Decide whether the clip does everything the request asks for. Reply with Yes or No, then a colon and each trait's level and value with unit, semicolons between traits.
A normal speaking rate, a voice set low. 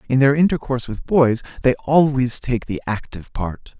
Yes: average, 175 wpm; low, 130 Hz